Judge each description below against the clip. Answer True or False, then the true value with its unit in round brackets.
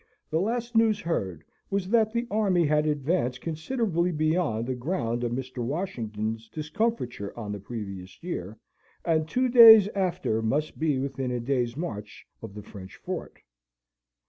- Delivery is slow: False (150 wpm)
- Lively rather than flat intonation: True (8.3 semitones)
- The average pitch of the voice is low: False (150 Hz)